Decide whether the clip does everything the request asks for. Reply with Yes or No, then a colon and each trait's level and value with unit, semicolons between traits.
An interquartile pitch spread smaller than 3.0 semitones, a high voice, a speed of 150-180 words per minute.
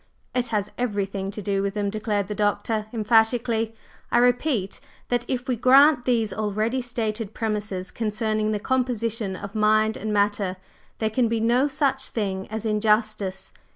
Yes: narrow, 2.5 semitones; high, 220 Hz; average, 155 wpm